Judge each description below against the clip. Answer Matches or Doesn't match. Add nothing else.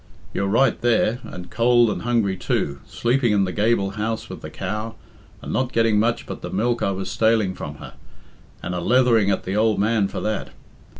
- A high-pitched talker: Doesn't match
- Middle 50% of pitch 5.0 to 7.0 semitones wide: Doesn't match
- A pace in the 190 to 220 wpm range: Matches